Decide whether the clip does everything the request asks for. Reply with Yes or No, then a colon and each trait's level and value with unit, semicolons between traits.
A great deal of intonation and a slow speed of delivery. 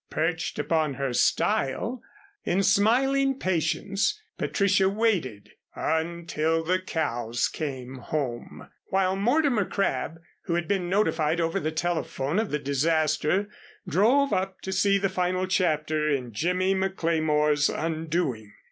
No: average, 4.2 semitones; slow, 120 wpm